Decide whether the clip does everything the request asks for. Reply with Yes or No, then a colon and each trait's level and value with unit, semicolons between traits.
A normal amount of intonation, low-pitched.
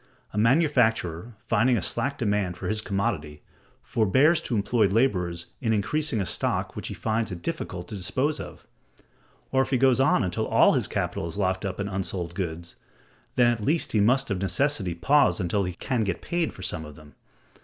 No: wide, 5.9 semitones; low, 105 Hz